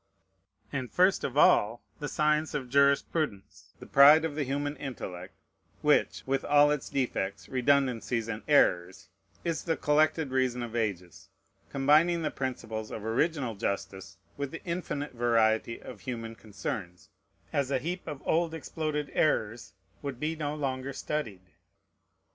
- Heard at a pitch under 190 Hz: Yes, low, 135 Hz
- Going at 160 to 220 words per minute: No, average, 140 wpm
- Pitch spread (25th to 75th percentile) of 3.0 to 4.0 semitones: No, average, 4.8 semitones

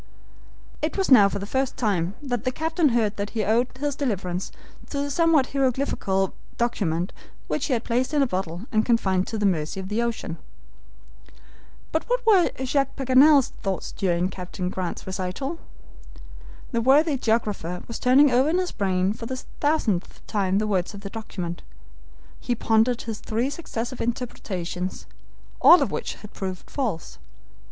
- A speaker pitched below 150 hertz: No, high, 225 Hz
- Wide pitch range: Yes, wide, 5.9 semitones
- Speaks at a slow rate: No, average, 165 wpm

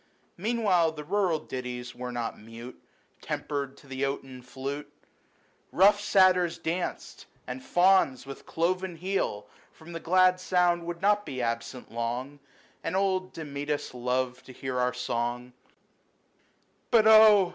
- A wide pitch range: Yes, wide, 6.5 semitones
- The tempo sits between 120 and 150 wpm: Yes, slow, 135 wpm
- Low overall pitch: No, medium, 150 Hz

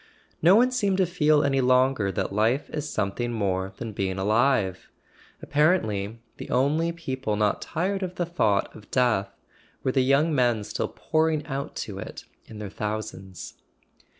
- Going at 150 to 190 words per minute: Yes, average, 165 wpm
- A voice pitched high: No, low, 125 Hz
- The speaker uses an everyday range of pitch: No, wide, 6.8 semitones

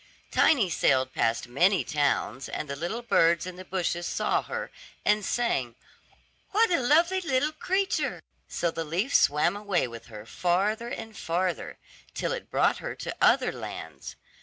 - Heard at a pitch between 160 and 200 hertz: Yes, medium, 185 Hz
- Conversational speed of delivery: Yes, average, 160 wpm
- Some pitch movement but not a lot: No, wide, 8.0 semitones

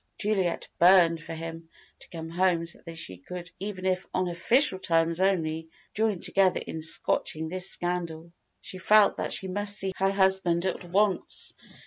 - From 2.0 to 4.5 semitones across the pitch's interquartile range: Yes, narrow, 2.5 semitones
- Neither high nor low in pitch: Yes, medium, 180 Hz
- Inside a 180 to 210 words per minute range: No, average, 165 wpm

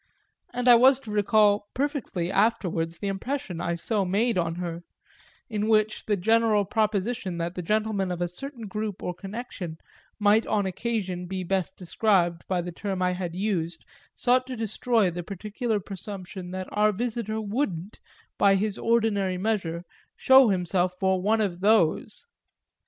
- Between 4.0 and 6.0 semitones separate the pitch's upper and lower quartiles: No, average, 3.5 semitones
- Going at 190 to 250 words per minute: No, average, 155 wpm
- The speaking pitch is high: Yes, high, 200 Hz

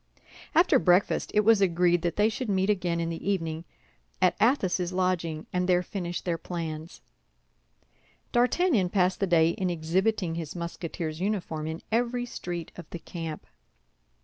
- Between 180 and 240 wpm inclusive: No, average, 150 wpm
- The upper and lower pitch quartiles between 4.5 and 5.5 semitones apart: No, average, 3.2 semitones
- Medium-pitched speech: Yes, medium, 180 Hz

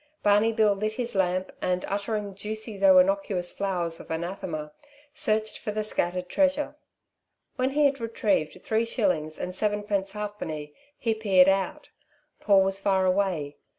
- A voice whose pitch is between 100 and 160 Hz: No, high, 200 Hz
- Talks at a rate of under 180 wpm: Yes, average, 150 wpm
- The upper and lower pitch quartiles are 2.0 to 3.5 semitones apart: Yes, average, 3.1 semitones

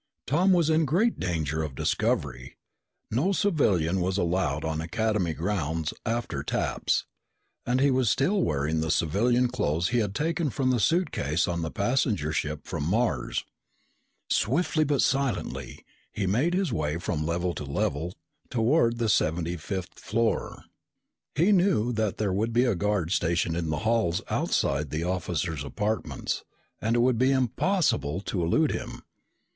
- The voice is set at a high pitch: No, low, 105 Hz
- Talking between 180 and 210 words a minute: No, average, 155 wpm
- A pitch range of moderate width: No, wide, 7.6 semitones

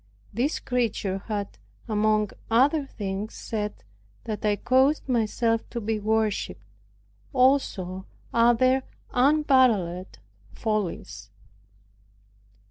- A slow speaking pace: Yes, slow, 85 wpm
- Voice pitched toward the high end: Yes, high, 225 Hz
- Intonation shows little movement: No, average, 3.6 semitones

